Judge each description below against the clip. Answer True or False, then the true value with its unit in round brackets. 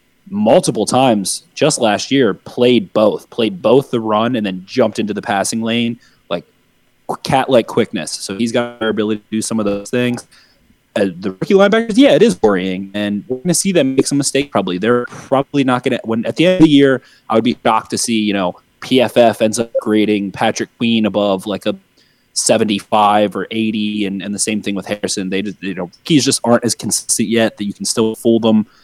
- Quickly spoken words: True (220 wpm)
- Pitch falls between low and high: False (110 Hz)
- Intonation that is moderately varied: True (3.6 semitones)